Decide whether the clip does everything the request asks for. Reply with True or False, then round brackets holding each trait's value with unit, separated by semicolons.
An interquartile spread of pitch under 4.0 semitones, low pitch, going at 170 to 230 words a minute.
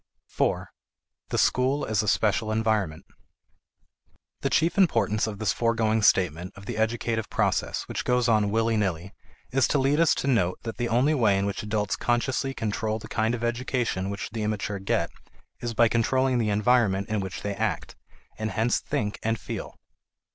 True (2.7 semitones; 110 Hz; 175 wpm)